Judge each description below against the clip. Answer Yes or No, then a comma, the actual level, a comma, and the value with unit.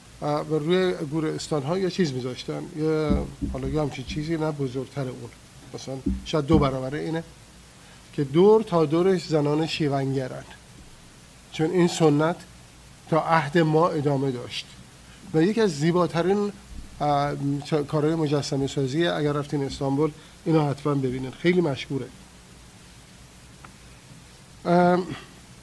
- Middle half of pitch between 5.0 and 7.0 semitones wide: No, average, 3.8 semitones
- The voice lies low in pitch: No, medium, 150 Hz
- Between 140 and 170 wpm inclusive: No, average, 110 wpm